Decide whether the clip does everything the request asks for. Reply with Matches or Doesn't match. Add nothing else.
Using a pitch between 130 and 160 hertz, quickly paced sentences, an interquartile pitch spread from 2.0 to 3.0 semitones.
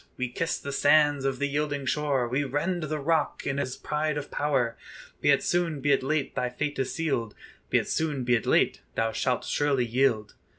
Matches